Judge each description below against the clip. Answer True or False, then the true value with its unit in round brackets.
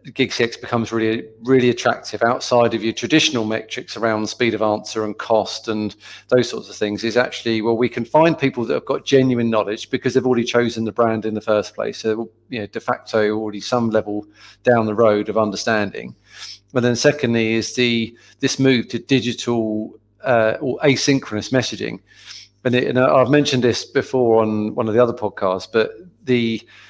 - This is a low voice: True (115 Hz)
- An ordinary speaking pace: True (190 wpm)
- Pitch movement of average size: False (2.3 semitones)